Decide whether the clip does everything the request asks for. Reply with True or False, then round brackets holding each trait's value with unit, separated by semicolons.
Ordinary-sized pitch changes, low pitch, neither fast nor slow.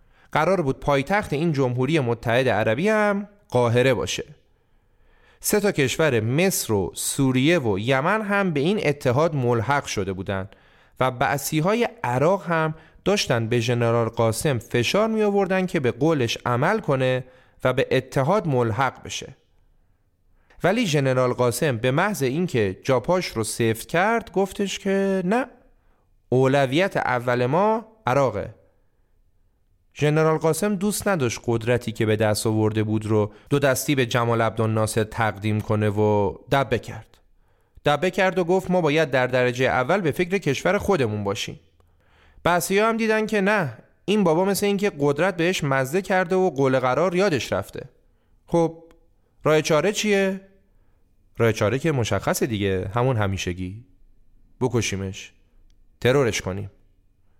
False (8.9 semitones; 130 Hz; 135 wpm)